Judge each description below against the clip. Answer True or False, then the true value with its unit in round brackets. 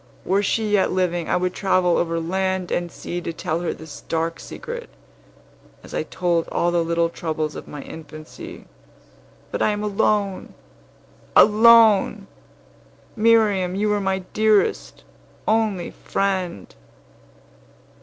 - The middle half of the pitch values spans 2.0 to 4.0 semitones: True (3.7 semitones)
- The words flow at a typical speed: False (130 wpm)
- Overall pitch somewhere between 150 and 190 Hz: True (185 Hz)